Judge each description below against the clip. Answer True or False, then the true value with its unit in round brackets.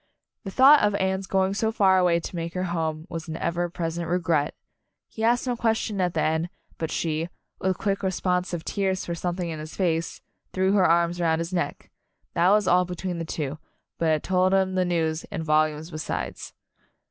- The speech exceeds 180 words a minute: True (195 wpm)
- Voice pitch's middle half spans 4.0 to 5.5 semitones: False (2.5 semitones)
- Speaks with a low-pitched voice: False (175 Hz)